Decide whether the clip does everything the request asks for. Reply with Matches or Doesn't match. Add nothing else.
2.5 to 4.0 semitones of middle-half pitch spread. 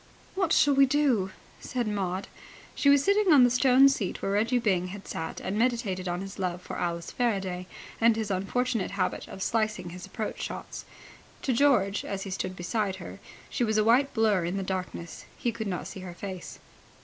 Doesn't match